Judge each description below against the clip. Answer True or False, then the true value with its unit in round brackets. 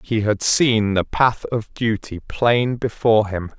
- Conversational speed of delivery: True (165 wpm)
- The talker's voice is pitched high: False (110 Hz)